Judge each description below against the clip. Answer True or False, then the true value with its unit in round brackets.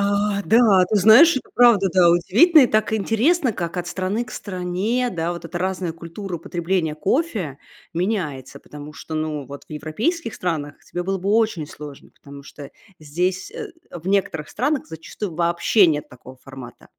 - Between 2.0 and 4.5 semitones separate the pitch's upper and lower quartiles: False (5.4 semitones)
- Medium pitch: True (180 Hz)